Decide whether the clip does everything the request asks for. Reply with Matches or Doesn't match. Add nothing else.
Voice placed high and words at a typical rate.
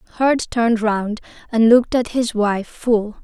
Matches